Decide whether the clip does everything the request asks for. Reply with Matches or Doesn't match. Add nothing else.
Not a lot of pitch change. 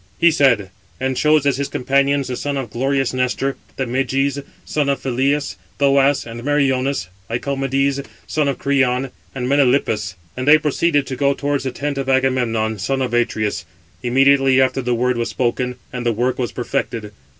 Matches